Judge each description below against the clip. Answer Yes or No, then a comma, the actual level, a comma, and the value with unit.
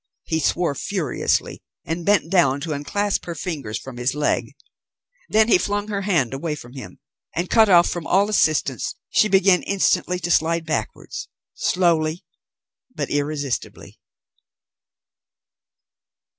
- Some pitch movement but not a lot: Yes, average, 4.7 semitones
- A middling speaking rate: No, slow, 130 wpm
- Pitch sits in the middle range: Yes, medium, 165 Hz